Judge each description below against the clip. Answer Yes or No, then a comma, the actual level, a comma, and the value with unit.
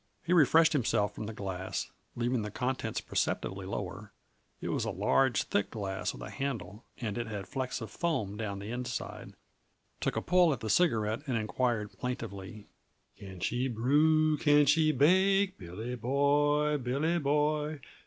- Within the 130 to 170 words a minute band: Yes, average, 160 wpm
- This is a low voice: Yes, low, 125 Hz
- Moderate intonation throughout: No, wide, 5.9 semitones